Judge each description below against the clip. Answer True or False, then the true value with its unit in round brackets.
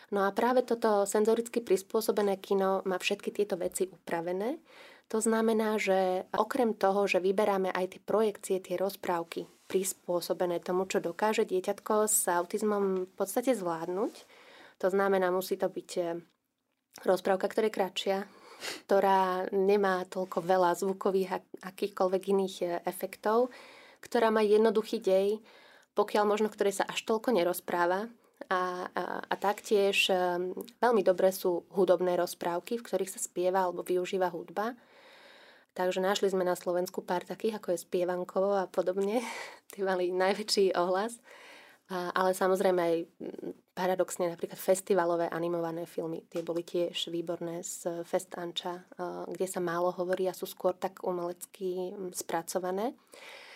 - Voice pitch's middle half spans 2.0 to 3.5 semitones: True (2.9 semitones)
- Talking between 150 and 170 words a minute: False (135 wpm)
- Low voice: False (190 Hz)